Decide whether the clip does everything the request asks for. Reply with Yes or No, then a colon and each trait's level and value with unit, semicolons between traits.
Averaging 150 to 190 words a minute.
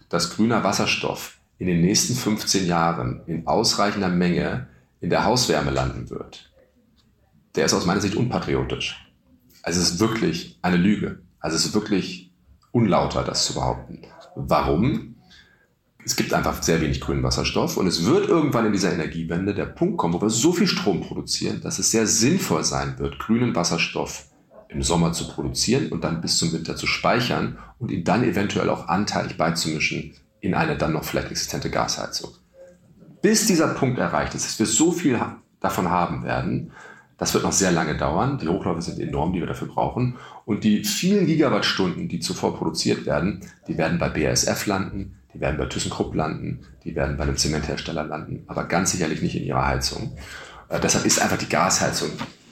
Yes: average, 175 wpm